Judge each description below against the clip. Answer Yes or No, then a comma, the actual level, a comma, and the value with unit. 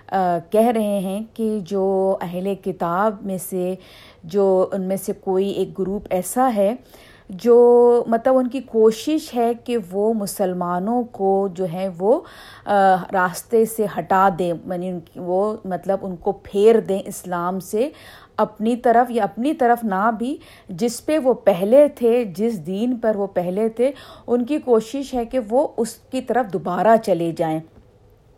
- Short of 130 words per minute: No, average, 165 wpm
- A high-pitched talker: Yes, high, 200 Hz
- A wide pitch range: No, average, 3.9 semitones